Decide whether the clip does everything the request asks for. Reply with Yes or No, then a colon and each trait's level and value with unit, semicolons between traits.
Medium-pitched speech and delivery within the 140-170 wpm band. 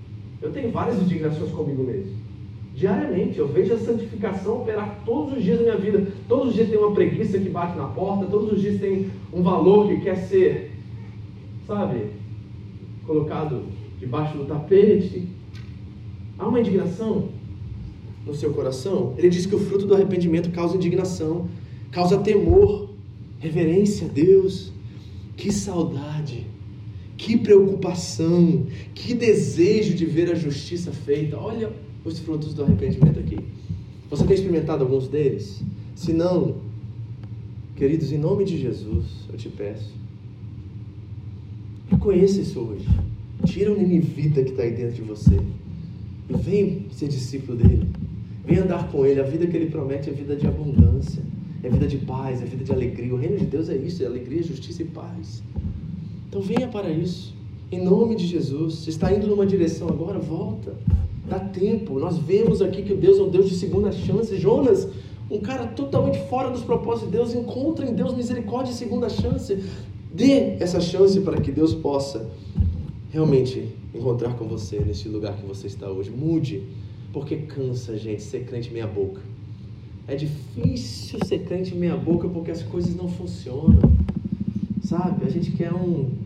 Yes: medium, 145 Hz; average, 160 wpm